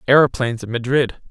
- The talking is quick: No, average, 140 wpm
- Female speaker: No, male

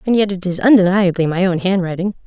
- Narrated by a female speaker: Yes, female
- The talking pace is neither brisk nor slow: No, fast, 210 wpm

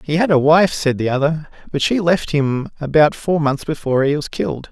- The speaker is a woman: No, male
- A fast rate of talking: Yes, fast, 230 wpm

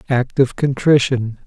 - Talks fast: No, slow, 125 wpm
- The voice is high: No, low, 130 Hz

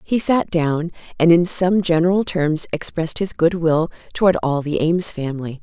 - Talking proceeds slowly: No, average, 180 wpm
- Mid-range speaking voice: Yes, medium, 165 Hz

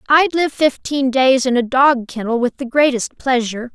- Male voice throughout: No, female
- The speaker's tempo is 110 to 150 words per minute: No, average, 190 wpm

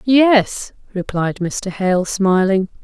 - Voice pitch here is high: Yes, high, 200 Hz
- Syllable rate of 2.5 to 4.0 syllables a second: Yes, 2.9 syllables/s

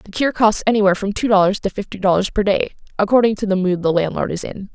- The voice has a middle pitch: No, high, 200 Hz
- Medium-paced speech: No, fast, 255 wpm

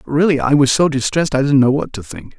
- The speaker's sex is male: Yes, male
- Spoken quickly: Yes, fast, 275 wpm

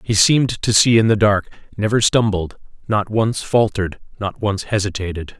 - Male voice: Yes, male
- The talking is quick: No, average, 165 wpm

